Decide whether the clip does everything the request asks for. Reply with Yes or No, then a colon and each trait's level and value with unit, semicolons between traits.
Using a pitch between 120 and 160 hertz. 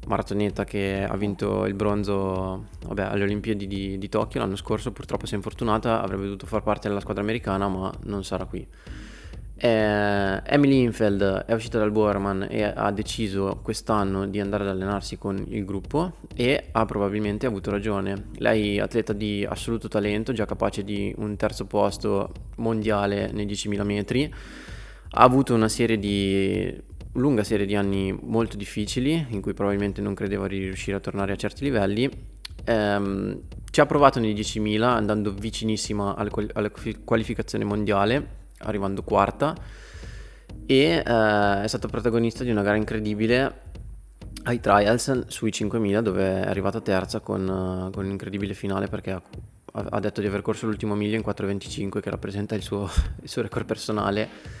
No: low, 105 Hz